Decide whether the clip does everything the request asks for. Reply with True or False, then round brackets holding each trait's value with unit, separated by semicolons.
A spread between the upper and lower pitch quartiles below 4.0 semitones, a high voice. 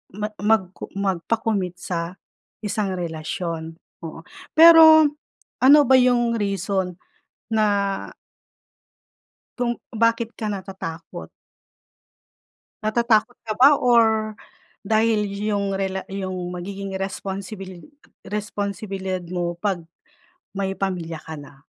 True (3.2 semitones; 200 Hz)